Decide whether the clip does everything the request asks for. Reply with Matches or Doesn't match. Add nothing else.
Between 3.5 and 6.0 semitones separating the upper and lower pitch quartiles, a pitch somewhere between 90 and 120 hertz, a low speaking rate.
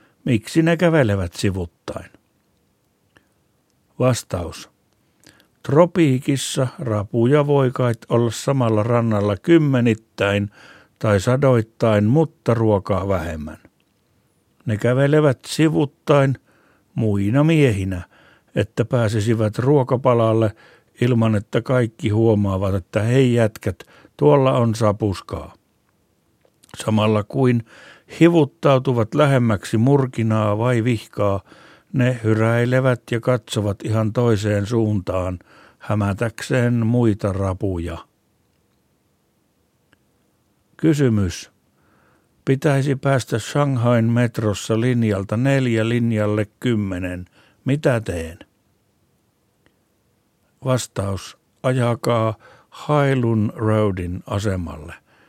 Matches